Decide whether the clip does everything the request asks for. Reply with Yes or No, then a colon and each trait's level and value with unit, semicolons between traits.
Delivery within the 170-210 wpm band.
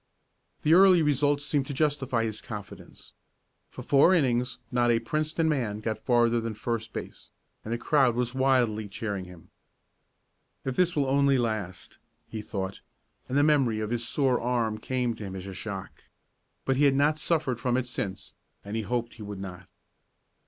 Yes: average, 180 wpm